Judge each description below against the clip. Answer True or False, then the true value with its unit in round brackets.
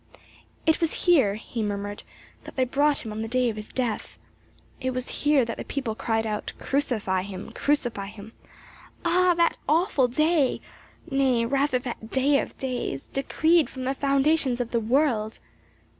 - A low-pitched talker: False (255 Hz)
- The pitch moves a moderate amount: True (4.4 semitones)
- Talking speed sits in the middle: True (165 wpm)